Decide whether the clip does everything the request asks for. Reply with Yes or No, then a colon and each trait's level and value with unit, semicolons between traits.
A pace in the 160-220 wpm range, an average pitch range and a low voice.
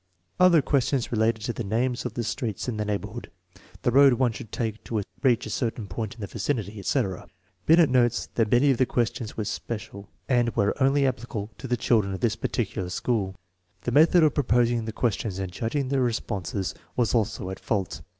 Yes: average, 200 wpm; average, 3.2 semitones; low, 115 Hz